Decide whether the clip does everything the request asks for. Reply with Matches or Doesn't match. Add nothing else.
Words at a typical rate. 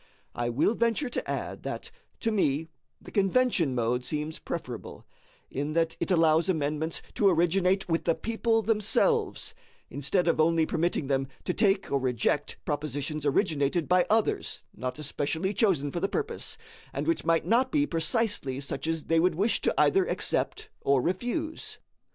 Matches